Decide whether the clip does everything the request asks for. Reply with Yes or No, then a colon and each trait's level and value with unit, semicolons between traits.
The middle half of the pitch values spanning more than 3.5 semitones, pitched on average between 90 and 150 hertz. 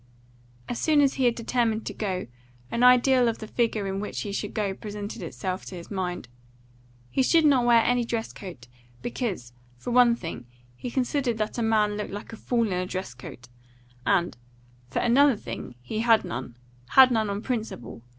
No: average, 4.1 semitones; high, 220 Hz